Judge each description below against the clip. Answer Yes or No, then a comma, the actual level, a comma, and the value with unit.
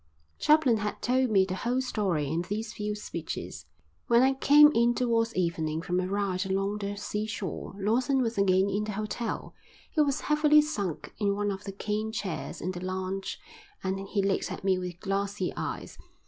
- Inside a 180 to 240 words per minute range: Yes, average, 185 wpm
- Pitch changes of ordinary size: Yes, average, 3.5 semitones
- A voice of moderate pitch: No, high, 205 Hz